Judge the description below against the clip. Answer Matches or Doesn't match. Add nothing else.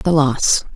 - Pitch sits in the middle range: Matches